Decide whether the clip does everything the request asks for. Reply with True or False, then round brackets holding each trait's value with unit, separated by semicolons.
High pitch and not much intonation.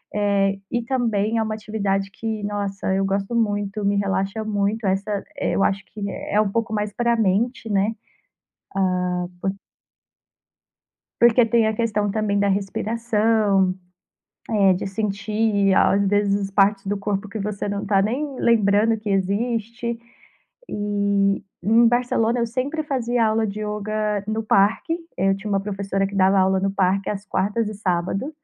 True (205 Hz; 2.1 semitones)